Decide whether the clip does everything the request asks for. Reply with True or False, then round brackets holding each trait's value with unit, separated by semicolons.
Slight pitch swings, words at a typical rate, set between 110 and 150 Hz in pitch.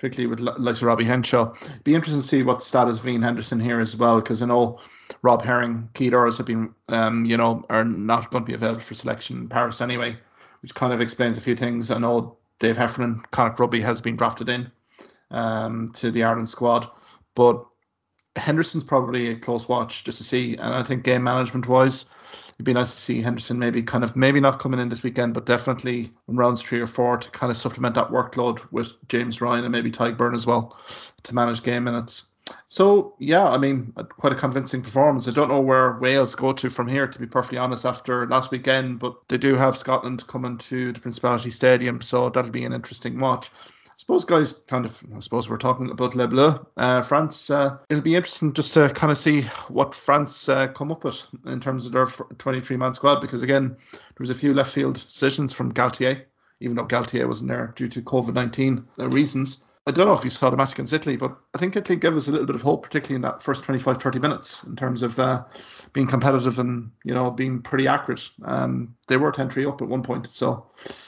False (2.0 semitones; 225 wpm; 125 Hz)